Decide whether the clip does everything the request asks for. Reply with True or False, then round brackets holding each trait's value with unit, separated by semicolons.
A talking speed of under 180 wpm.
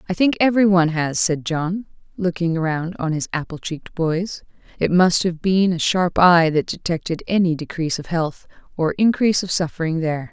False (185 wpm)